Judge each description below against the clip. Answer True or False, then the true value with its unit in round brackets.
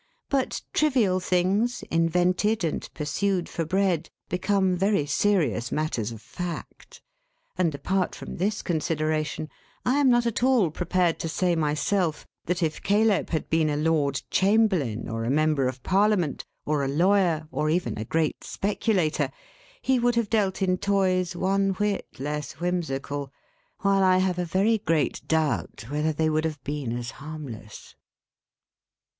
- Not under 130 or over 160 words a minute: True (150 wpm)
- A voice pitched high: False (175 Hz)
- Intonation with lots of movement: False (4.4 semitones)